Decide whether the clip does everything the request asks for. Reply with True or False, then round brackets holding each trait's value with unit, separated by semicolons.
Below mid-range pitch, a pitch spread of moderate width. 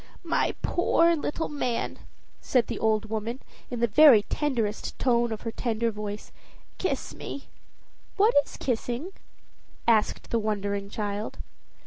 False (230 Hz; 3.8 semitones)